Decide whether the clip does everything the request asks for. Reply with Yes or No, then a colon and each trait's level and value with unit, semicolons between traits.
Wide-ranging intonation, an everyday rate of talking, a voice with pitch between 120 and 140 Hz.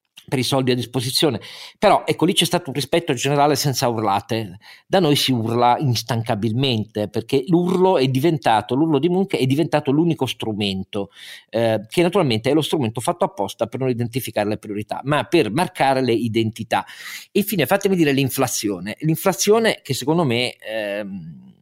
Yes: wide, 6.2 semitones; average, 160 wpm; low, 135 Hz